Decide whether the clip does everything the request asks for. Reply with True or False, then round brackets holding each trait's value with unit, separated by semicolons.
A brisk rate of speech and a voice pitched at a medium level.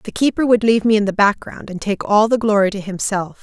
False (265 wpm; 210 Hz)